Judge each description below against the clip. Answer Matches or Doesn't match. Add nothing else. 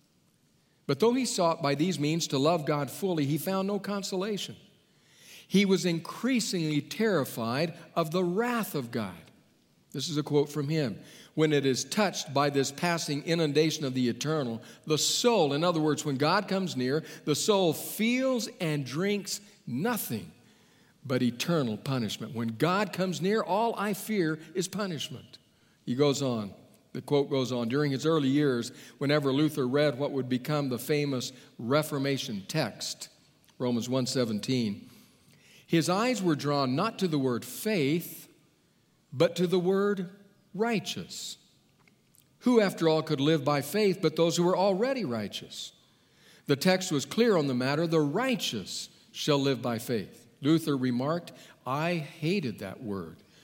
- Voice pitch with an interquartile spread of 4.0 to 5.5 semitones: Matches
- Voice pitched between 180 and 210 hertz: Doesn't match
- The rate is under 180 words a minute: Matches